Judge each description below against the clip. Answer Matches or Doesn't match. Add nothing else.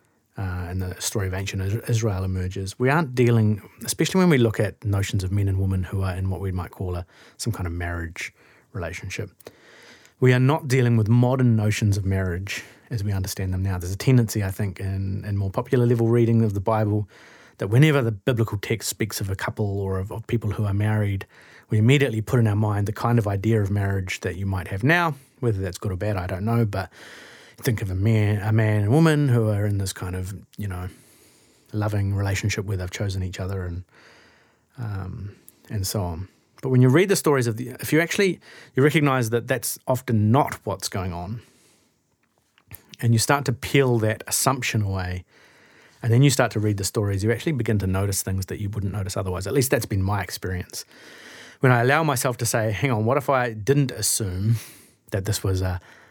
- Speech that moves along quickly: Matches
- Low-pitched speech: Matches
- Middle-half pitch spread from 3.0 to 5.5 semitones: Matches